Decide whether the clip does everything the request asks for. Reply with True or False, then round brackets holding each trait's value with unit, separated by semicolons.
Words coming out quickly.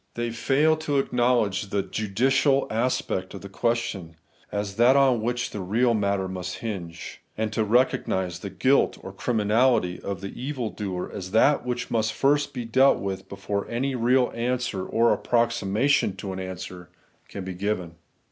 False (165 wpm)